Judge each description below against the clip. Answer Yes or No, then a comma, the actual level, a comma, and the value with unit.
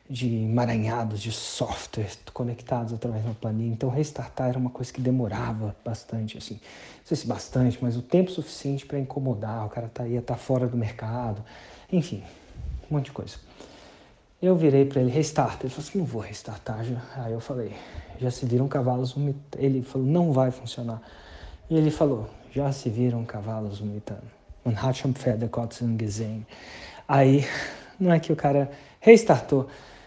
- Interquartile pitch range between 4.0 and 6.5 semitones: No, average, 3.5 semitones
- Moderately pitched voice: No, low, 125 Hz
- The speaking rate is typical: Yes, average, 160 wpm